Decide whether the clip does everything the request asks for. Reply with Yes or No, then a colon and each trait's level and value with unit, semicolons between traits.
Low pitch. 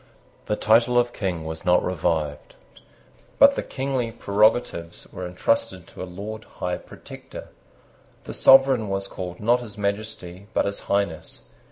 Yes: low, 100 Hz